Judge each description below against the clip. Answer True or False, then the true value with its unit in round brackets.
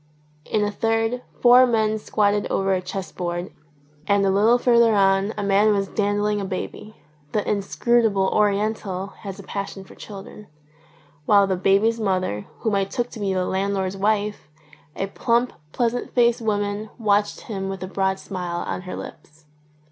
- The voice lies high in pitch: True (200 Hz)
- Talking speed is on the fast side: False (165 wpm)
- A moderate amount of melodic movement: False (2.1 semitones)